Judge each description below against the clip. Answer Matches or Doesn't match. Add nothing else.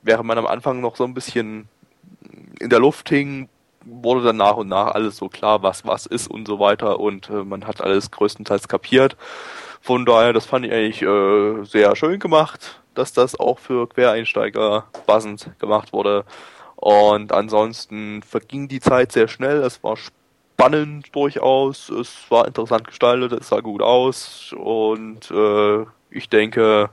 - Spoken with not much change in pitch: Doesn't match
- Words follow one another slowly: Doesn't match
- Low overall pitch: Matches